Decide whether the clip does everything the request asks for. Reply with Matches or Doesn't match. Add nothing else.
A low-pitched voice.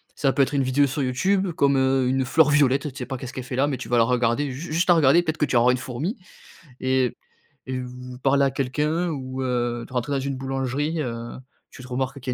Matches